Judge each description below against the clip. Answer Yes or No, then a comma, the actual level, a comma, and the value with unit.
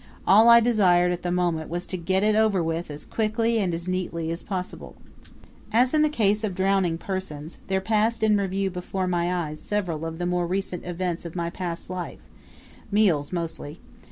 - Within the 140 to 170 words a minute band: No, average, 190 wpm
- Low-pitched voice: No, medium, 185 Hz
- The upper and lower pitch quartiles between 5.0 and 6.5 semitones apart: No, average, 3.3 semitones